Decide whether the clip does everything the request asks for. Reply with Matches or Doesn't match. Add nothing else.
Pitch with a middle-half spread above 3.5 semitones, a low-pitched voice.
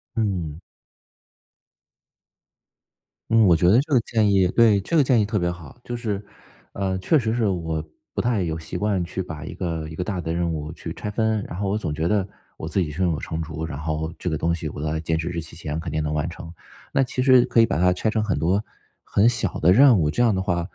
Matches